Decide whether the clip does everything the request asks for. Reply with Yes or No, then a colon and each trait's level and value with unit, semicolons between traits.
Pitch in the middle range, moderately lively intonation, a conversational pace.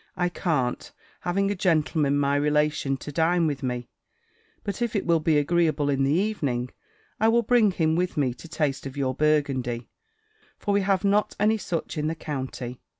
Yes: medium, 155 Hz; average, 4.7 semitones; average, 185 wpm